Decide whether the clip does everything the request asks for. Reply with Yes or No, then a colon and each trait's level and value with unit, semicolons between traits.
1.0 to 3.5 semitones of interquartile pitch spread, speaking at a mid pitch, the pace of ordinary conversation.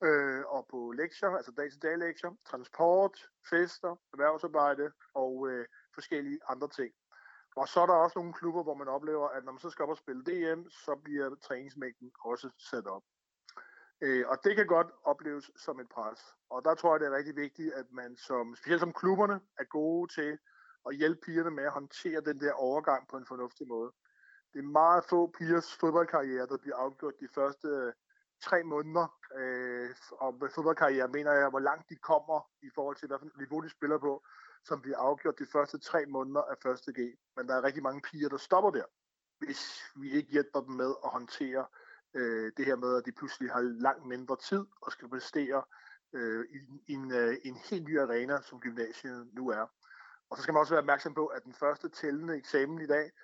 No: average, 3.9 semitones; medium, 145 Hz; average, 200 wpm